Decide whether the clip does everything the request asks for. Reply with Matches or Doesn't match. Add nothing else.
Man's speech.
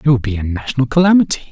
Matches